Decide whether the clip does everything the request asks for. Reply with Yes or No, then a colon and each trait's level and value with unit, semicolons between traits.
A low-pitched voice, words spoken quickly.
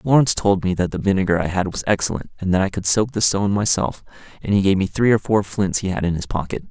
Yes: very low, 95 Hz; fast, 275 wpm